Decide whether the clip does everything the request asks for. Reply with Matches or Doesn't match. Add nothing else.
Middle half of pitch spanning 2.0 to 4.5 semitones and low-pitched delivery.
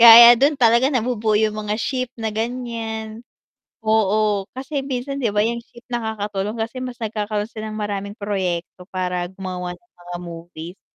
Doesn't match